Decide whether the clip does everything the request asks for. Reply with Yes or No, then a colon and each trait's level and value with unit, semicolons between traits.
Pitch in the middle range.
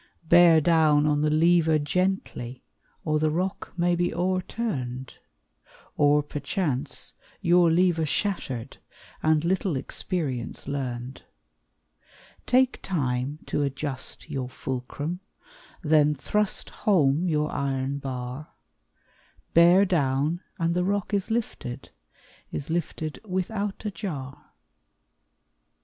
Yes: medium, 155 Hz